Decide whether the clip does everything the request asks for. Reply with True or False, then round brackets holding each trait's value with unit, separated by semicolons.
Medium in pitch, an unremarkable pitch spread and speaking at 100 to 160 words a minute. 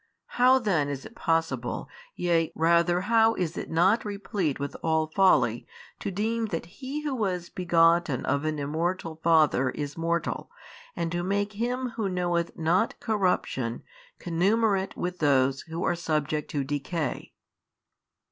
True (170 Hz; 4.2 semitones; 145 wpm)